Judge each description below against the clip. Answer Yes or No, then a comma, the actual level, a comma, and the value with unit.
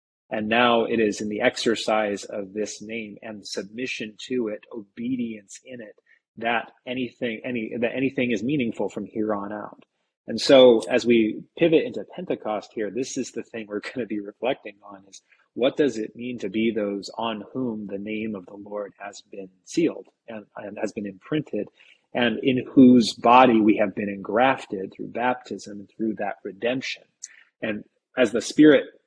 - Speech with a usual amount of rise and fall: Yes, average, 3.0 semitones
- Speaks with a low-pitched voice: Yes, low, 110 Hz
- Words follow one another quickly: No, average, 180 wpm